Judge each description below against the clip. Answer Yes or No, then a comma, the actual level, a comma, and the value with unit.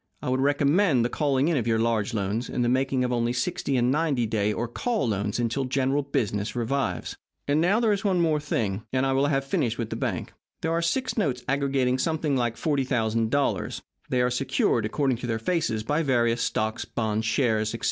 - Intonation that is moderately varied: Yes, average, 3.7 semitones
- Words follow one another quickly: Yes, fast, 210 wpm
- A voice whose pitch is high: No, low, 125 Hz